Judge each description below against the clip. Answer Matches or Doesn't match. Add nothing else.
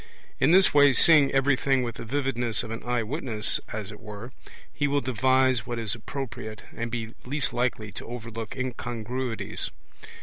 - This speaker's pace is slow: Doesn't match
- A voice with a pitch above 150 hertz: Doesn't match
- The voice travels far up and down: Doesn't match